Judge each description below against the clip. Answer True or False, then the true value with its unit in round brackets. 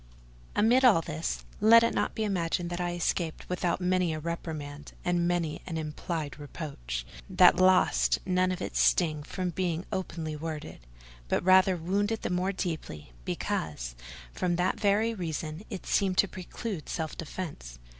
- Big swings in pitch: False (3.0 semitones)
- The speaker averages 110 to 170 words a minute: True (160 wpm)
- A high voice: False (175 Hz)